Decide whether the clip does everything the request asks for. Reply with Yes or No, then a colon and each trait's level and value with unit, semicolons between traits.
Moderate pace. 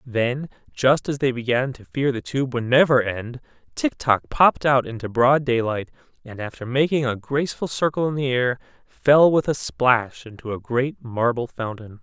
Yes: average, 185 wpm